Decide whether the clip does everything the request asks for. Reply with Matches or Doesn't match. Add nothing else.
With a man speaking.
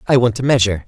Matches